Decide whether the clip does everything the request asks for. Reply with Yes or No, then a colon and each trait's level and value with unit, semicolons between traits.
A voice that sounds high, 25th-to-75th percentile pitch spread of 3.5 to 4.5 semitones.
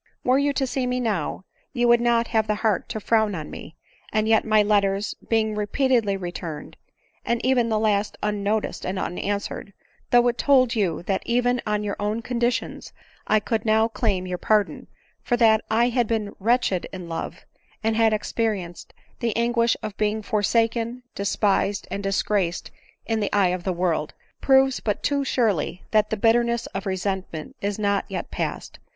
No: high, 215 Hz; average, 2.8 semitones